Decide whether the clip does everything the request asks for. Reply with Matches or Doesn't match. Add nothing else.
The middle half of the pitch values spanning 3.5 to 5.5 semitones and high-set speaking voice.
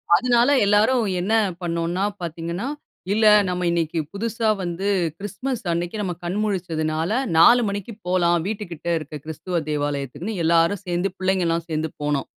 Doesn't match